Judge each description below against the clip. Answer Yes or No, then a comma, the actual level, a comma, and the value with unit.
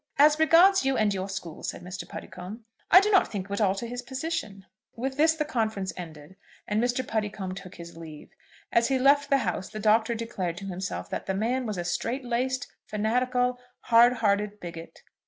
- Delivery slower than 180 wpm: No, average, 195 wpm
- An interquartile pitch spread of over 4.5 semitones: Yes, average, 5.1 semitones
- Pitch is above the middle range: Yes, high, 220 Hz